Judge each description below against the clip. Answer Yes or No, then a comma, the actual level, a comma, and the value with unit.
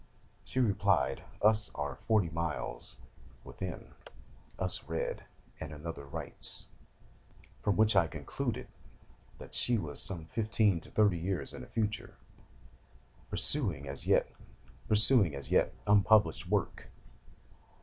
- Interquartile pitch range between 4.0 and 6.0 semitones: Yes, average, 5.1 semitones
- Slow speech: Yes, slow, 115 wpm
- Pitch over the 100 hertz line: No, very low, 95 Hz